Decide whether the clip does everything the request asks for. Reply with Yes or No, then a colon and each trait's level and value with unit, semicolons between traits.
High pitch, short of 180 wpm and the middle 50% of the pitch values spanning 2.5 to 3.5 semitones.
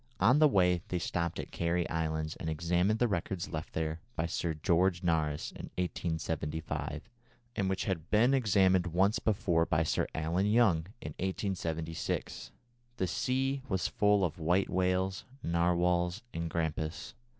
No: very low, 85 Hz; average, 150 wpm; average, 2.9 semitones